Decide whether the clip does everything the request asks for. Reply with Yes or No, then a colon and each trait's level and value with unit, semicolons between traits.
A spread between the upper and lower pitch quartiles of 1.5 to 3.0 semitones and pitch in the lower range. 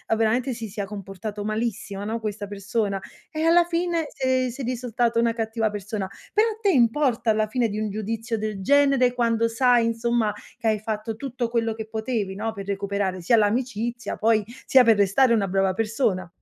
No: average, 2.7 semitones; high, 225 Hz